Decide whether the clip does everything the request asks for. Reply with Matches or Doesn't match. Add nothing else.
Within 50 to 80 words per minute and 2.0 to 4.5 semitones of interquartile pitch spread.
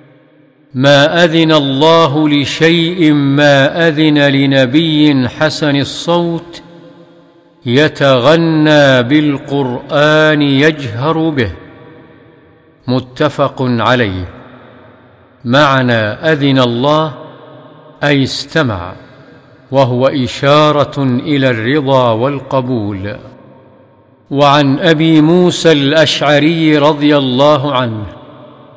Matches